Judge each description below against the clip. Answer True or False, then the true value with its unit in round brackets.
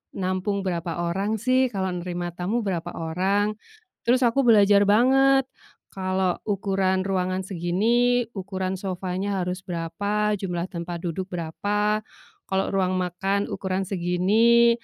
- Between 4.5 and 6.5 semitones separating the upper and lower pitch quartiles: False (2.6 semitones)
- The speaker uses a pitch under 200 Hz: True (190 Hz)